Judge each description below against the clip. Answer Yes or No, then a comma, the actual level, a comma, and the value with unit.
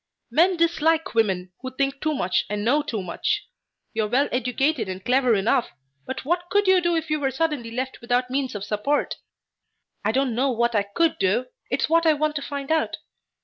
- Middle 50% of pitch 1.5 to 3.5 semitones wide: No, wide, 5.4 semitones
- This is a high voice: Yes, very high, 265 Hz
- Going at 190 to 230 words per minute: Yes, fast, 205 wpm